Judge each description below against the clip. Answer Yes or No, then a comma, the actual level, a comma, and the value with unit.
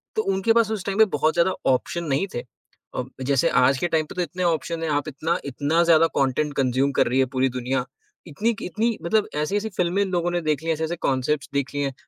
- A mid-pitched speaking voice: Yes, medium, 160 Hz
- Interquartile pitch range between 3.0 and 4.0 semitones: No, average, 4.7 semitones